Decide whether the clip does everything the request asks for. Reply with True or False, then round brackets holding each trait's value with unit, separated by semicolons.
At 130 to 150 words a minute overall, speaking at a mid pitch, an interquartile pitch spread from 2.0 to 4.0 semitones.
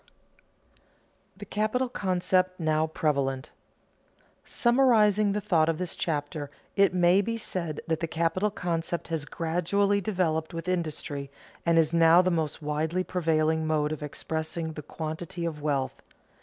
True (140 wpm; 165 Hz; 2.9 semitones)